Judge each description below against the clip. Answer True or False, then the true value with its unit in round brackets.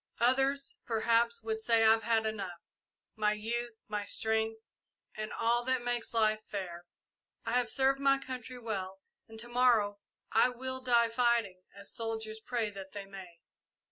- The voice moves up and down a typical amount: False (2.2 semitones)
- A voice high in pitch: True (225 Hz)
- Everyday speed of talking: True (155 wpm)